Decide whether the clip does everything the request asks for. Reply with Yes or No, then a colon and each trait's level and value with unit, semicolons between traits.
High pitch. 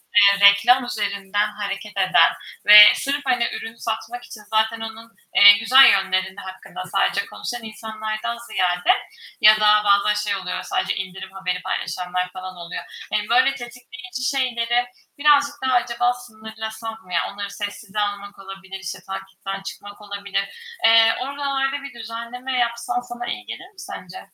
Yes: high, 215 Hz